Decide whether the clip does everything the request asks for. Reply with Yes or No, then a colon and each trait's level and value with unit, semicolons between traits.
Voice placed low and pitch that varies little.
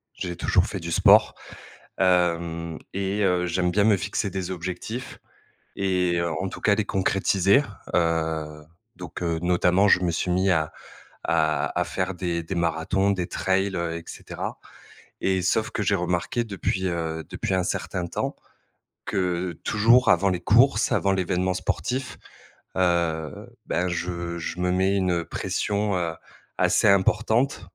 Yes: very low, 90 Hz; narrow, 2.3 semitones